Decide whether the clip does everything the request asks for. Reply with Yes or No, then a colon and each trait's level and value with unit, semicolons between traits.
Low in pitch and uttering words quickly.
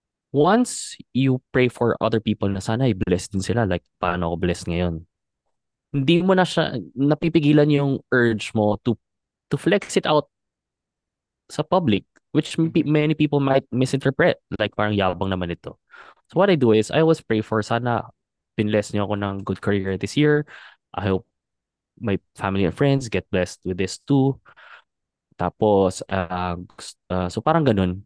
Yes: low, 110 Hz; fast, 165 wpm